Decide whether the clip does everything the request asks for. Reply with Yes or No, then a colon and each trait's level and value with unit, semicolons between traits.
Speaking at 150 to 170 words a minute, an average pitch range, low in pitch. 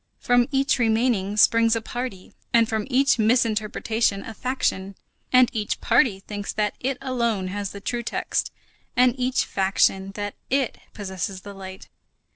No: average, 155 wpm; average, 3.6 semitones; high, 220 Hz